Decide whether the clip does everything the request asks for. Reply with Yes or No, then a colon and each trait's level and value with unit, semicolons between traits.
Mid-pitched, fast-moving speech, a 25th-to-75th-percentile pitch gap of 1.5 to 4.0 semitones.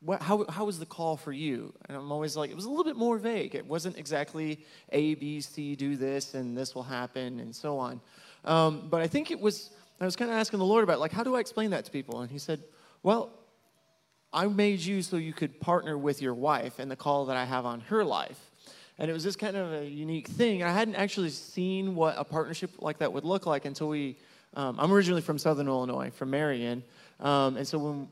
No: medium, 155 Hz; fast, 245 wpm; average, 5.3 semitones